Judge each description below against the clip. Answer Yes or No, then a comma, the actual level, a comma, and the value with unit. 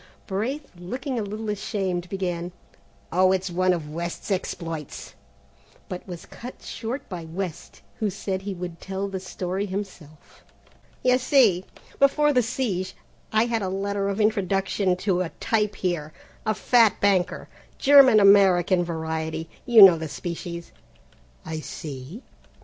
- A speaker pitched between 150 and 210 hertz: Yes, high, 190 Hz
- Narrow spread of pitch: No, average, 3.4 semitones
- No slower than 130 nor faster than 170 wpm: Yes, average, 140 wpm